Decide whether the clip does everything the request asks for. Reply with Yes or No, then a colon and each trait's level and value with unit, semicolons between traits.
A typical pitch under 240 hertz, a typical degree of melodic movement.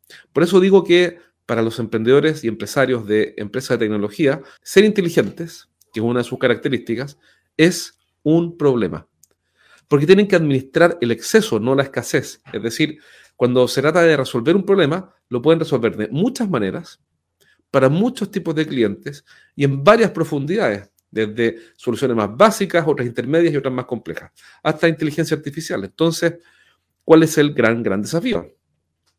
No: medium, 140 Hz; wide, 6.5 semitones